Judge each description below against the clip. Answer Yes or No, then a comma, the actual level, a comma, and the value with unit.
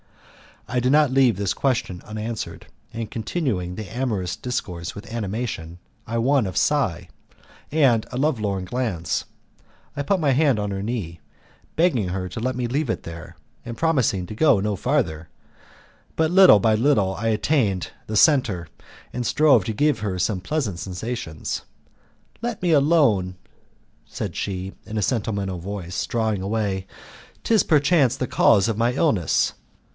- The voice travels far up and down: Yes, wide, 5.9 semitones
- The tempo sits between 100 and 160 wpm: Yes, average, 155 wpm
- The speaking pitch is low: Yes, low, 110 Hz